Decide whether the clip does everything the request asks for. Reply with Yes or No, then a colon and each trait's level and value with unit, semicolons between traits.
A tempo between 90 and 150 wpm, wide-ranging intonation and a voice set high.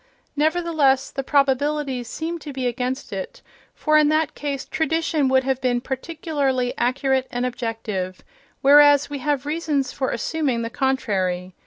No: average, 145 wpm; average, 3.1 semitones; very high, 270 Hz